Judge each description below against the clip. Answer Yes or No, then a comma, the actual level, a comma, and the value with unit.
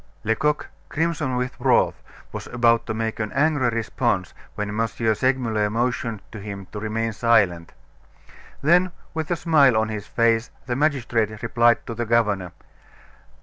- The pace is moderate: Yes, average, 145 wpm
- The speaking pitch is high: No, low, 115 Hz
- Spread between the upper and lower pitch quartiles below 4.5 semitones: Yes, average, 3.1 semitones